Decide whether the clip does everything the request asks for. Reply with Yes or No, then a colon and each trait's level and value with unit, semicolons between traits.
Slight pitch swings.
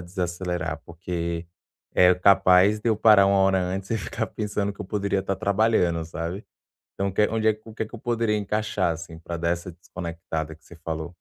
No: average, 3.5 semitones